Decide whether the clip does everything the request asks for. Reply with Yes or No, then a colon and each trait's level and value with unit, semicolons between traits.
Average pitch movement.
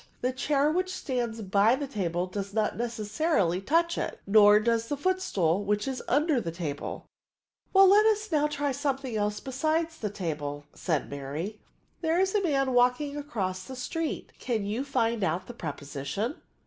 No: wide, 6.8 semitones